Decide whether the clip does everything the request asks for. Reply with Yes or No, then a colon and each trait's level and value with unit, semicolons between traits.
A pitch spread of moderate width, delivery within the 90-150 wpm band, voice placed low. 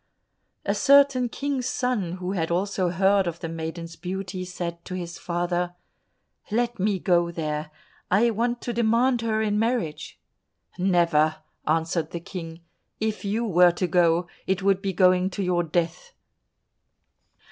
No: average, 4.2 semitones; average, 145 wpm; medium, 185 Hz